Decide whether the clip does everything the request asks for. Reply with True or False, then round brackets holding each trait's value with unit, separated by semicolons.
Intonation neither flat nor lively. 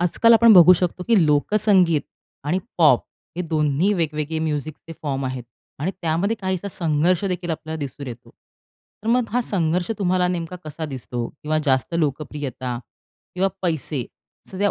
True (3.9 semitones)